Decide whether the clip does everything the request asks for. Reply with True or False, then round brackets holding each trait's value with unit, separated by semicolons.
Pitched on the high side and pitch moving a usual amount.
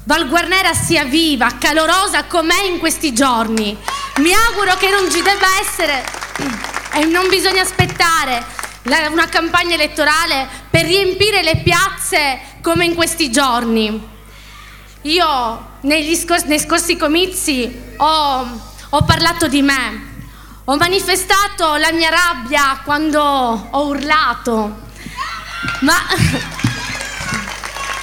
True (320 Hz; 4.0 semitones)